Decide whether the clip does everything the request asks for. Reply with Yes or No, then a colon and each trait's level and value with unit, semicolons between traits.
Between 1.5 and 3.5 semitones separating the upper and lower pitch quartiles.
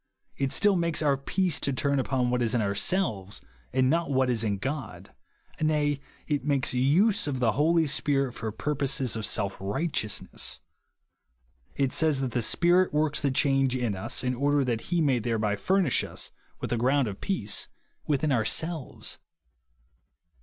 No: average, 3.9 semitones